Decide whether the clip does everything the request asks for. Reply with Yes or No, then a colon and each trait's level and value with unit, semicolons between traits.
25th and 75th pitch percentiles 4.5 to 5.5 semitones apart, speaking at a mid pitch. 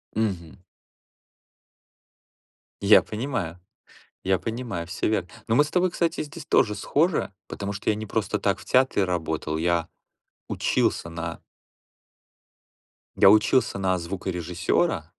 No: average, 4.8 semitones; low, 100 Hz